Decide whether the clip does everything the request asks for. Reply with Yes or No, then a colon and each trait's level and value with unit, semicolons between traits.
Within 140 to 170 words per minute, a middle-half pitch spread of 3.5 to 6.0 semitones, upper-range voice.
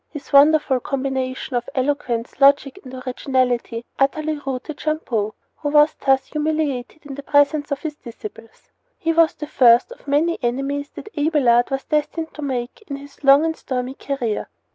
No: average, 165 wpm; average, 2.9 semitones; very high, 275 Hz